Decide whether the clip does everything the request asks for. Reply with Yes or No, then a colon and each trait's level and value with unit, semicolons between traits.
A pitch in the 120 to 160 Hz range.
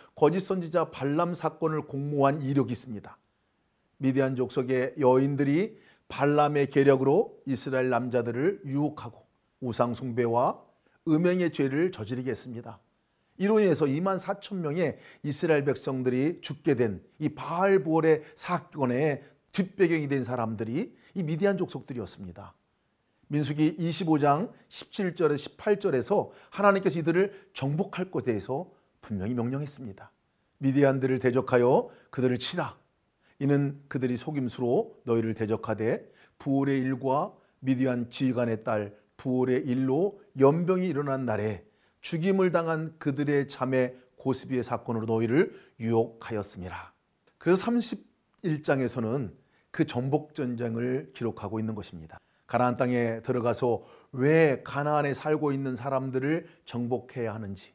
Yes: low, 135 Hz